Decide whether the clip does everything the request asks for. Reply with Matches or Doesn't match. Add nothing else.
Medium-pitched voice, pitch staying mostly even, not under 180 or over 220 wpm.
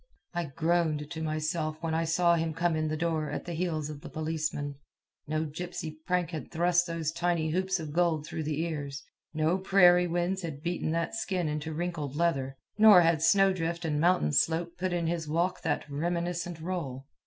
Matches